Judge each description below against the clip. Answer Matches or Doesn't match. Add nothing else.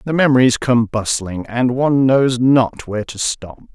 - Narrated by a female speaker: Doesn't match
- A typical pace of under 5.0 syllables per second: Matches